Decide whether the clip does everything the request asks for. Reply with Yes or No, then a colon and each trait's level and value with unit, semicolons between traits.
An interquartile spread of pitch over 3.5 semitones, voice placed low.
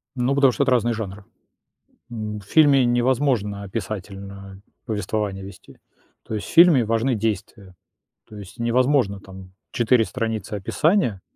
Yes: average, 4.1 semitones; low, 110 Hz